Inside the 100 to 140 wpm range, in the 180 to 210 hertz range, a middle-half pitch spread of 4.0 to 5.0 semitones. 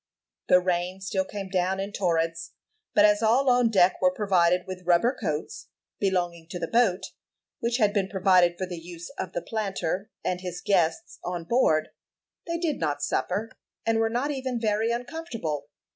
No: average, 175 wpm; high, 190 Hz; average, 4.3 semitones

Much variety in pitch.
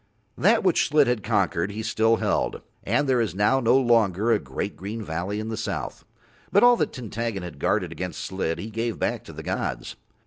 No: average, 3.4 semitones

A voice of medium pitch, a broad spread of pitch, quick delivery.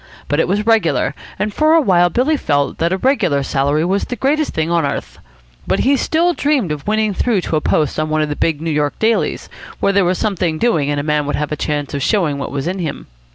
Yes: medium, 170 Hz; wide, 6.6 semitones; fast, 250 wpm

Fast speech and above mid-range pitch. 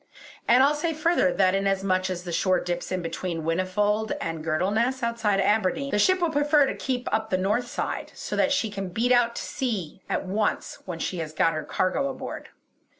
Yes: fast, 210 wpm; high, 205 Hz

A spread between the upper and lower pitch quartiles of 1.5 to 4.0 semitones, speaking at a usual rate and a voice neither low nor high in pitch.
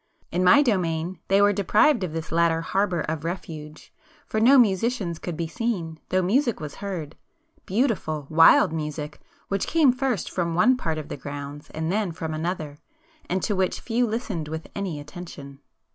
No: average, 4.9 semitones; average, 170 wpm; medium, 175 Hz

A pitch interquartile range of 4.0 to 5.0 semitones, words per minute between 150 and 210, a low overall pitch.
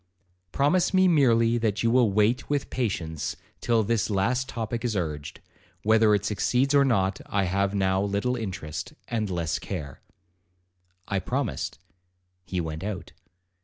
No: average, 4.5 semitones; average, 140 wpm; low, 105 Hz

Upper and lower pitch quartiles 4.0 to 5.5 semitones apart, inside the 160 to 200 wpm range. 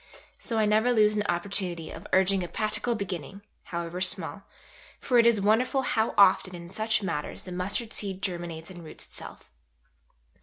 No: average, 3.6 semitones; average, 165 wpm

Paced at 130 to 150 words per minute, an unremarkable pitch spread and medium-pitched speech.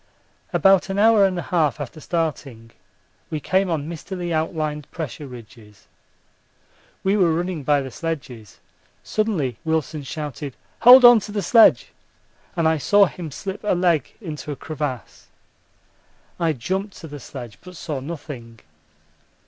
Yes: average, 145 wpm; average, 4.7 semitones; medium, 160 Hz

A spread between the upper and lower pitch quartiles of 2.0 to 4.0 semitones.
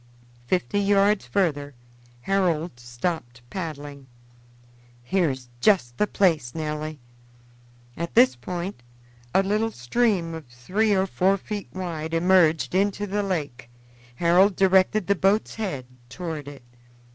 No: average, 5.2 semitones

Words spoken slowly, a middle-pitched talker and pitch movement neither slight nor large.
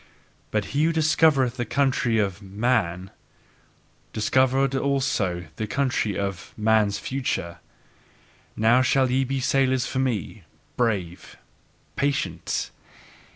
No: slow, 110 wpm; low, 125 Hz; average, 4.8 semitones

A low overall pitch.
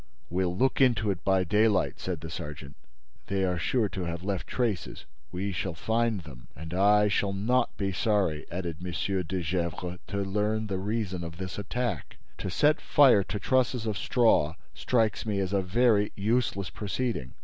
Yes: low, 100 Hz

